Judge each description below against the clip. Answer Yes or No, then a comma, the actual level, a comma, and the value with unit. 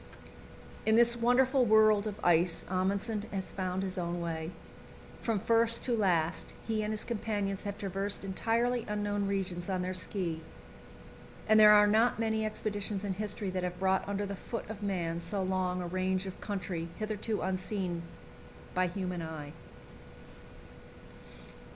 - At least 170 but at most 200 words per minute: No, average, 150 wpm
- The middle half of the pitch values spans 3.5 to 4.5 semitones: No, average, 2.8 semitones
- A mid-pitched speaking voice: No, high, 200 Hz